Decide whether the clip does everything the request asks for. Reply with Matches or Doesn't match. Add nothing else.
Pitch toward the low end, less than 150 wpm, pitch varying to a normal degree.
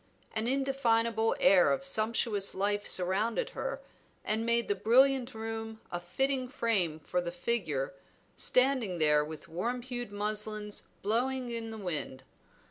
Doesn't match